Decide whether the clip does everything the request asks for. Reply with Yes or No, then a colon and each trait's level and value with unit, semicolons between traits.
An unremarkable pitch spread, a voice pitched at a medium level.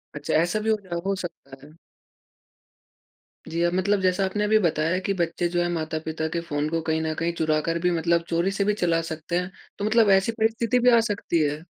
Yes: average, 3.6 semitones; medium, 175 Hz